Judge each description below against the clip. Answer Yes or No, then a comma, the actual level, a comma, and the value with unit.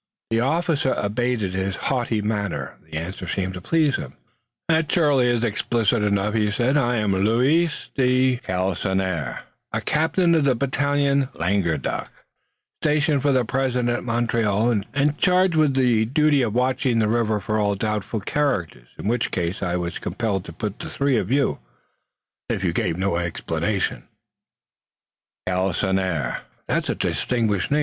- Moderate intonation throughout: No, wide, 5.7 semitones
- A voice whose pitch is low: Yes, low, 115 Hz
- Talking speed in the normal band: Yes, average, 155 wpm